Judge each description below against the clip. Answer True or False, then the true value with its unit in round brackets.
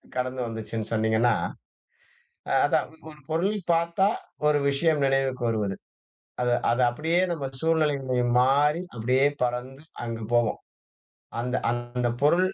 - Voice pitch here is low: True (130 Hz)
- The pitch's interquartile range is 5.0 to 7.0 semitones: False (4.1 semitones)